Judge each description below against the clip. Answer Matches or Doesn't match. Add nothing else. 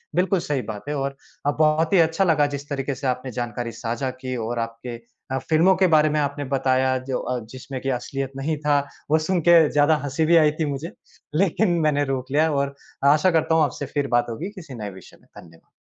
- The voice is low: Doesn't match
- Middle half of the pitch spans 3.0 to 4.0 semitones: Matches